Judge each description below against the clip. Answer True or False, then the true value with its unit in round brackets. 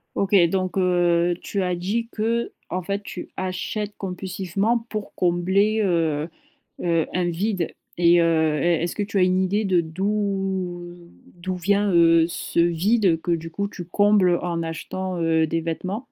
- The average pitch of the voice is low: False (180 Hz)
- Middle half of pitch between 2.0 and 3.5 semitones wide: True (2.8 semitones)